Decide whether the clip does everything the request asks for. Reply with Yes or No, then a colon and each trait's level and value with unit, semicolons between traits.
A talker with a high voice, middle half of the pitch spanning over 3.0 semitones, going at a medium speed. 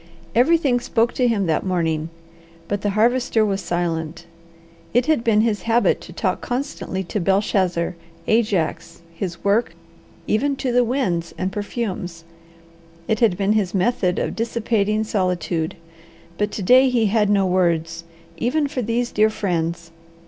Yes: high, 205 Hz; average, 4.7 semitones; average, 145 wpm